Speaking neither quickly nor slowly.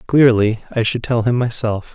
Yes: average, 185 wpm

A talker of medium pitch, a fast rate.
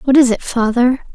No: high, 245 Hz; fast, 210 wpm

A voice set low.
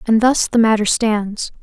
No: high, 220 Hz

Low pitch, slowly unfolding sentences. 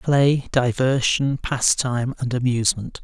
Yes: low, 130 Hz; slow, 100 wpm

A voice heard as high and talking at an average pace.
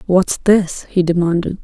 No: medium, 180 Hz; average, 145 wpm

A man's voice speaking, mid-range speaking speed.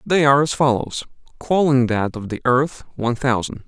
Yes: male; average, 180 wpm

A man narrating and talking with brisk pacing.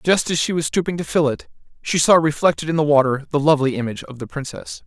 Yes: male; fast, 245 wpm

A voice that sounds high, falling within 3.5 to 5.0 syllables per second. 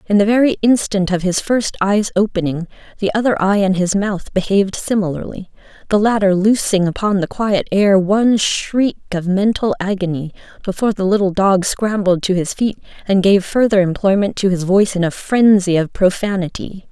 No: high, 195 Hz; 5.2 syllables/s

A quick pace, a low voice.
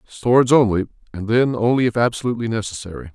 No: average, 150 wpm; low, 115 Hz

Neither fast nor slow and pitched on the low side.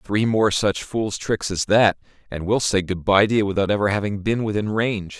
No: fast, 220 wpm; low, 105 Hz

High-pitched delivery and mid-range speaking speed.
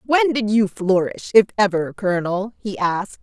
Yes: high, 205 Hz; average, 165 wpm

